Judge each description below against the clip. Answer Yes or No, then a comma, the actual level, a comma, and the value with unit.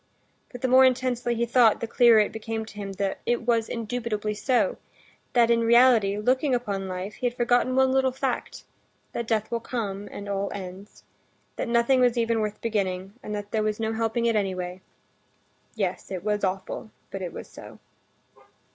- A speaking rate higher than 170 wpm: Yes, average, 180 wpm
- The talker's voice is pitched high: Yes, high, 225 Hz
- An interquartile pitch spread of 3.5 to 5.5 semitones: No, average, 3.1 semitones